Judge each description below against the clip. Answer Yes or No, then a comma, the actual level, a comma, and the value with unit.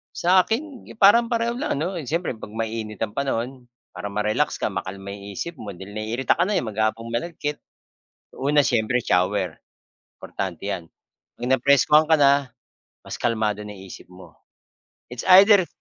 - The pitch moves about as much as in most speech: No, wide, 7.2 semitones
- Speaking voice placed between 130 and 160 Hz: No, low, 120 Hz